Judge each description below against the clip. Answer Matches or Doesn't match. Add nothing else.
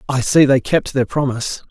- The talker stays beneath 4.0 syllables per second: Doesn't match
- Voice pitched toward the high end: Doesn't match